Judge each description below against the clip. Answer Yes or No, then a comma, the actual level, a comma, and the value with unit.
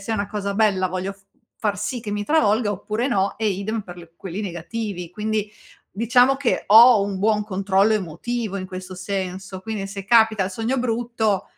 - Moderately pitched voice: No, high, 205 Hz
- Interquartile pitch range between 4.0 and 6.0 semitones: No, average, 2.7 semitones